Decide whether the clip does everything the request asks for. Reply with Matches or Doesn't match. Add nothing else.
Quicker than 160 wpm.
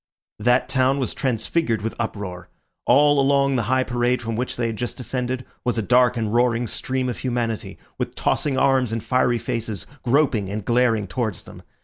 Matches